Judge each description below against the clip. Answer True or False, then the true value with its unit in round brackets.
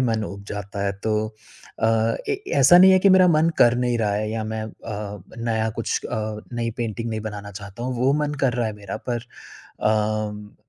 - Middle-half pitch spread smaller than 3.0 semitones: True (2.6 semitones)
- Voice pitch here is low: True (110 Hz)